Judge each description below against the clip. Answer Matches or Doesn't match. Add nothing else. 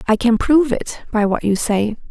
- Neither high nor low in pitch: Doesn't match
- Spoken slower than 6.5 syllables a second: Matches